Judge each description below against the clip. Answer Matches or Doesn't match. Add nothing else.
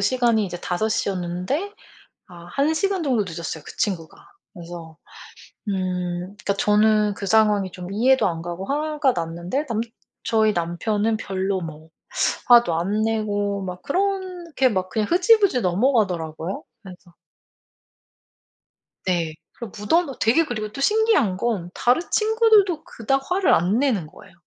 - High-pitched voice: Matches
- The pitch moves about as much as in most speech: Doesn't match